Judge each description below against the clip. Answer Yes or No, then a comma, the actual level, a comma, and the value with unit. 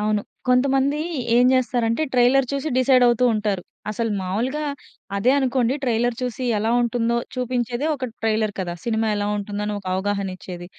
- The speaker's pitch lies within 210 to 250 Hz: Yes, high, 235 Hz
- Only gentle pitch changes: No, average, 3.4 semitones